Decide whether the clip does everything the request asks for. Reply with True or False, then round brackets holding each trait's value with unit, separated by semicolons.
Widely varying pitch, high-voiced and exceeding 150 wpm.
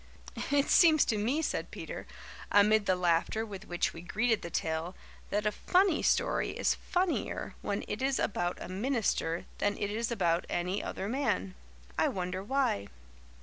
True (5.9 semitones; 205 Hz; 165 wpm)